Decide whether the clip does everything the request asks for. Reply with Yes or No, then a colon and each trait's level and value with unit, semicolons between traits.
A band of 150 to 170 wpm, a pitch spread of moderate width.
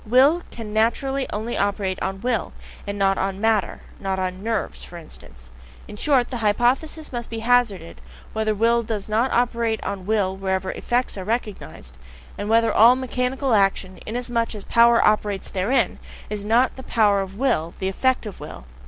No: average, 180 wpm; average, 3.8 semitones